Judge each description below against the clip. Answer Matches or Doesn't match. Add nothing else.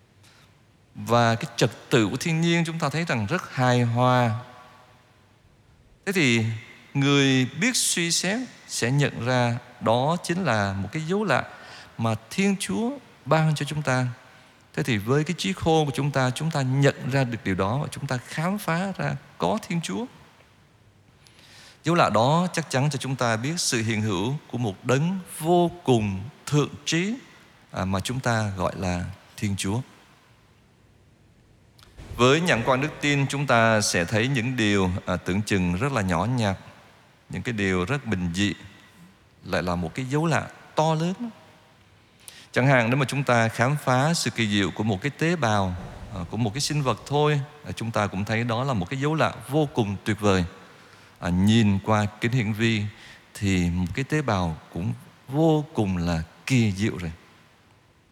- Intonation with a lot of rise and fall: Matches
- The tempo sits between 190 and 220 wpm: Doesn't match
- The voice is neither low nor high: Doesn't match